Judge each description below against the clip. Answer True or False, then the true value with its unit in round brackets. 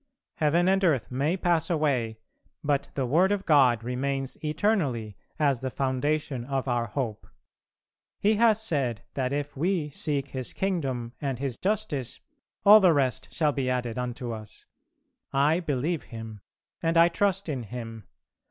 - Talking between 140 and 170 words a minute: True (150 wpm)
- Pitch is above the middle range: False (140 Hz)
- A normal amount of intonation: True (5.0 semitones)